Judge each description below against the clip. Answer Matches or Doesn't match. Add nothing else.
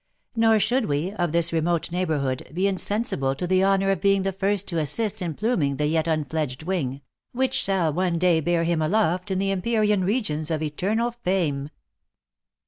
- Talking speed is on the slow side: Doesn't match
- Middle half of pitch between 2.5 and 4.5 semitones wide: Matches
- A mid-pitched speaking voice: Matches